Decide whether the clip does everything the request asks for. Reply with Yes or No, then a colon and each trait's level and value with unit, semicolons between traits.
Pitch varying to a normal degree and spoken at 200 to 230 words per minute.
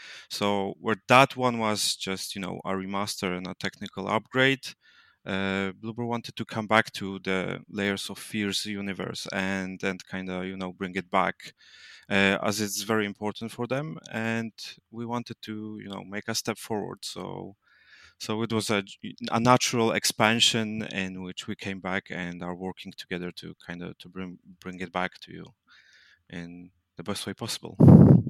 No: average, 3.1 semitones; average, 175 wpm